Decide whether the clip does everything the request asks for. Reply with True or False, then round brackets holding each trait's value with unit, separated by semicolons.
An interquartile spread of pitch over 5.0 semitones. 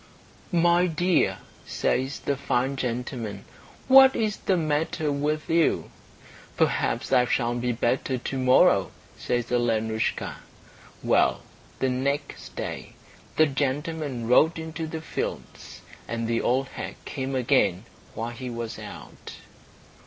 False (4.6 semitones)